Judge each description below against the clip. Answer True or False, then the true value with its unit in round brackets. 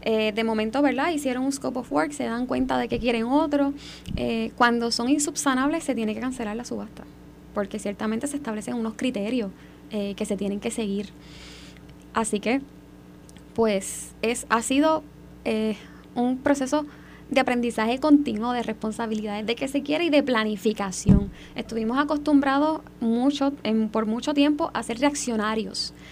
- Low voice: False (235 Hz)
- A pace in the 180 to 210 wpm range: False (160 wpm)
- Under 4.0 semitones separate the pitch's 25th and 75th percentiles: False (4.3 semitones)